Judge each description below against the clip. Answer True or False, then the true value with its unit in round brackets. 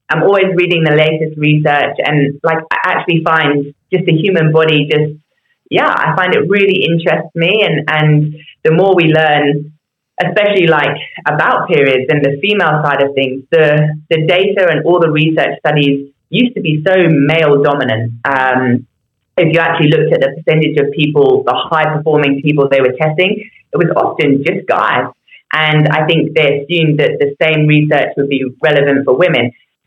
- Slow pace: False (180 wpm)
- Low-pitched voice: False (155 Hz)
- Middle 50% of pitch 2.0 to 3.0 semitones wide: True (2.6 semitones)